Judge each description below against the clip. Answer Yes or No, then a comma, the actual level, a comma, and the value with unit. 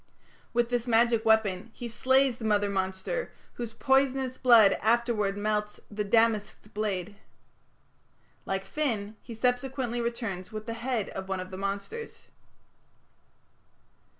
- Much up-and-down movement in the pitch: No, average, 3.1 semitones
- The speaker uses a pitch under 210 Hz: No, high, 225 Hz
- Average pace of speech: No, slow, 125 wpm